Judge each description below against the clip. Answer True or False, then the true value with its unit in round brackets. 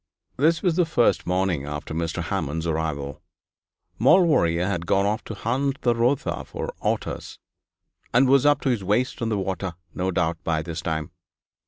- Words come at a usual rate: True (175 wpm)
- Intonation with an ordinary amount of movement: False (7.4 semitones)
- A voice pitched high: False (95 Hz)